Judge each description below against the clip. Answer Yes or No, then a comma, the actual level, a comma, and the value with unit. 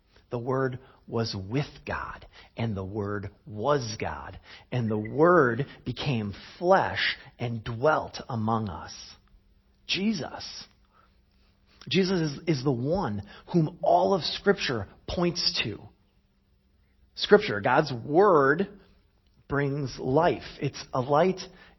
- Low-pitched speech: Yes, low, 130 Hz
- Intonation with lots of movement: Yes, wide, 7.7 semitones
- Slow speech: Yes, slow, 105 wpm